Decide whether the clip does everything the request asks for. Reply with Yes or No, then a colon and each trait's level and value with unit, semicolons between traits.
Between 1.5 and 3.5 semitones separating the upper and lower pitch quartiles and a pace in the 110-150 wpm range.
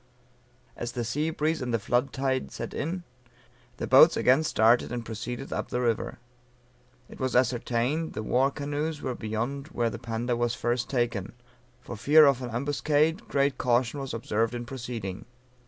No: average, 3.2 semitones; average, 170 wpm